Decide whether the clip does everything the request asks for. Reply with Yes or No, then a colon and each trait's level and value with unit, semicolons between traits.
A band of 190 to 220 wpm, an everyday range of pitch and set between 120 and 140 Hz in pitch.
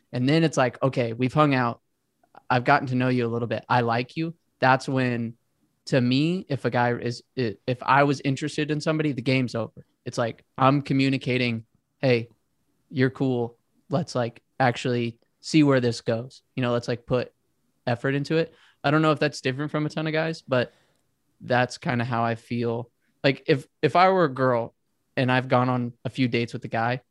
Yes: fast, 205 wpm; average, 3.0 semitones; low, 130 Hz